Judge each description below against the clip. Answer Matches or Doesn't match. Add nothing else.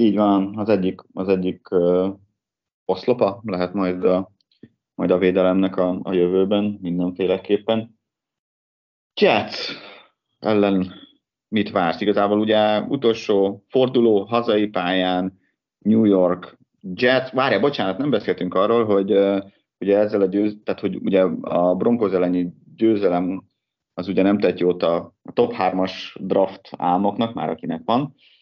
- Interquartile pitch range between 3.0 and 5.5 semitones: Doesn't match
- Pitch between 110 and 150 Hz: Doesn't match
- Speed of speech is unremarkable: Matches